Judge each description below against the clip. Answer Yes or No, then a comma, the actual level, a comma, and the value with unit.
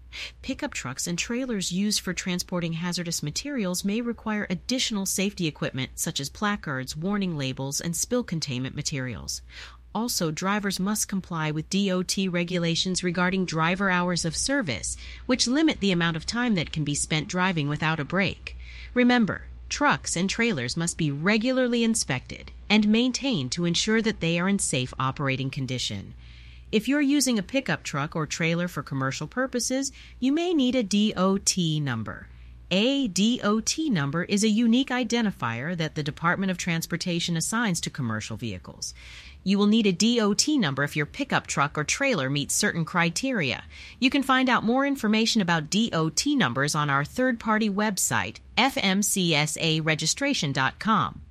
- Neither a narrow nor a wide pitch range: No, wide, 6.9 semitones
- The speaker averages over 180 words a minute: No, average, 150 wpm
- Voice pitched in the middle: Yes, medium, 180 Hz